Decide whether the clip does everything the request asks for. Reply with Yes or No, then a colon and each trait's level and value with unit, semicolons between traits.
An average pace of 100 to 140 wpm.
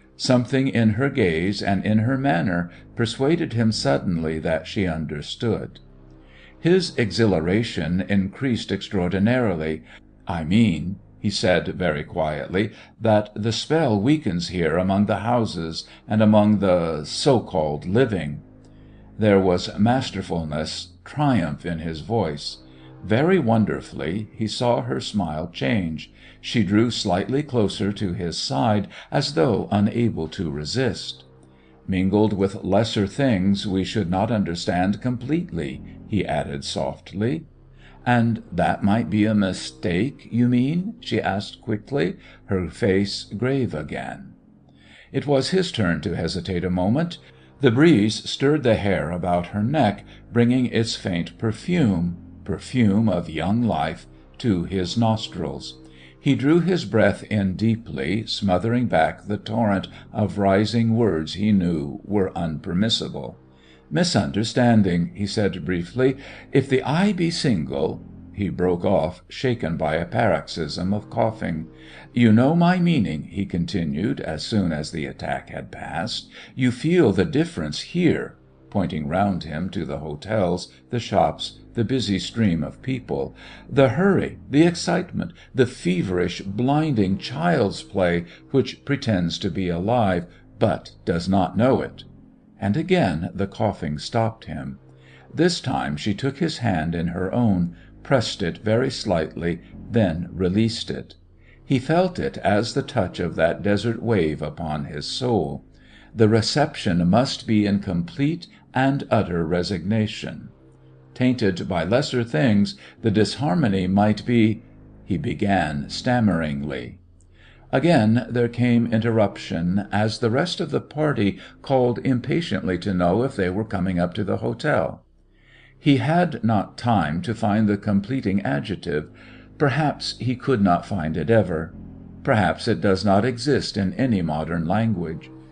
Yes: slow, 135 wpm